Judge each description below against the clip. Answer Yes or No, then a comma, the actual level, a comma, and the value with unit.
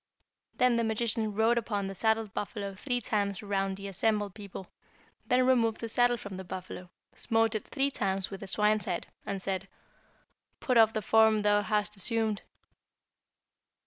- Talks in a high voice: Yes, high, 210 Hz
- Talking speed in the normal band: Yes, average, 165 wpm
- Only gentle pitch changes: Yes, narrow, 2.3 semitones